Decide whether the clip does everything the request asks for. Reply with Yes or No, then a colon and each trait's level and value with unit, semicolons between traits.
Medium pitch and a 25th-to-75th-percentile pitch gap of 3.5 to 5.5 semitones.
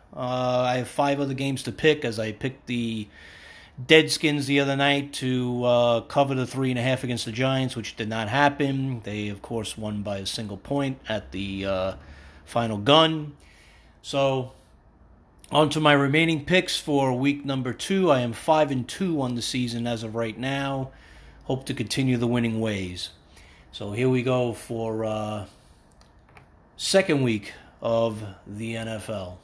No: low, 125 Hz; average, 4.1 semitones